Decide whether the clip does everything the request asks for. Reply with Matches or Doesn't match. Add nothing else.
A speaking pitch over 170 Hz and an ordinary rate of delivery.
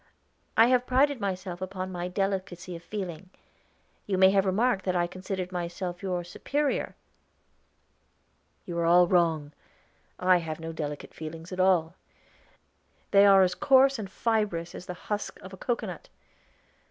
Matches